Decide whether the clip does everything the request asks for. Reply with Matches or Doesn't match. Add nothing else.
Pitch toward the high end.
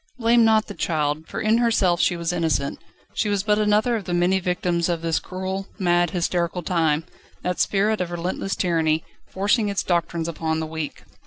Doesn't match